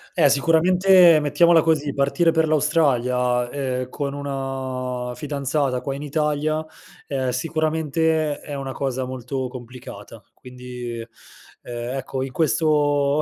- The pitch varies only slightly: No, average, 3.4 semitones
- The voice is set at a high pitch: No, medium, 140 Hz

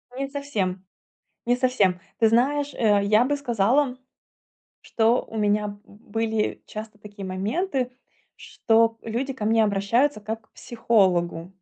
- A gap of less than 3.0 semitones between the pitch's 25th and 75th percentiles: No, average, 3.6 semitones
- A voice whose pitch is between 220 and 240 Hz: Yes, high, 225 Hz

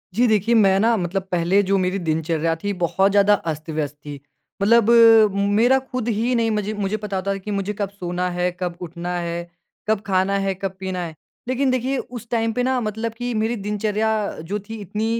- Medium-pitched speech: No, high, 200 Hz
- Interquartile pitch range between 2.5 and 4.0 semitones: Yes, average, 3.7 semitones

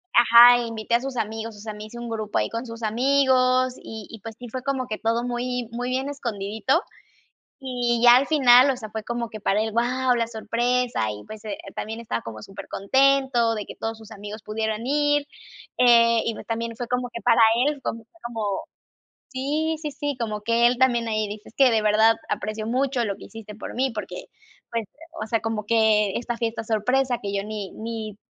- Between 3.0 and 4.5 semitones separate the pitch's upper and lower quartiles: No, narrow, 2.5 semitones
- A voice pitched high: Yes, high, 230 Hz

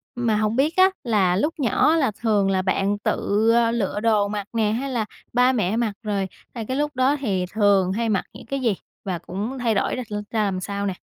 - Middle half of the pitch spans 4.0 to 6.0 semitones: No, average, 3.6 semitones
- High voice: Yes, high, 215 Hz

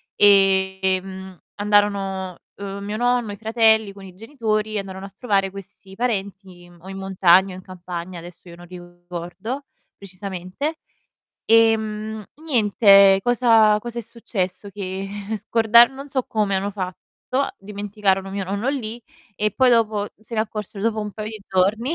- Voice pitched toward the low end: No, high, 200 Hz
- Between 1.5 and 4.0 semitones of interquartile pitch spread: Yes, narrow, 2.6 semitones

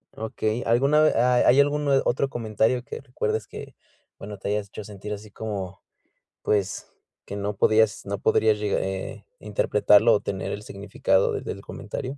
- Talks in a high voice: No, low, 110 Hz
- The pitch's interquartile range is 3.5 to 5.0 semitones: Yes, average, 3.8 semitones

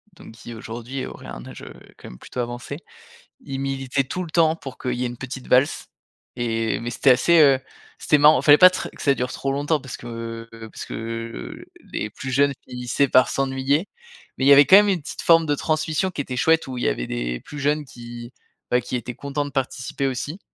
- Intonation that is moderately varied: Yes, average, 3.3 semitones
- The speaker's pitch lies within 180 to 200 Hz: No, low, 135 Hz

